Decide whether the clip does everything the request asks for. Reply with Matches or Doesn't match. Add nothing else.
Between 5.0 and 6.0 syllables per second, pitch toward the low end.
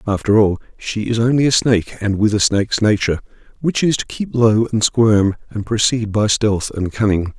Matches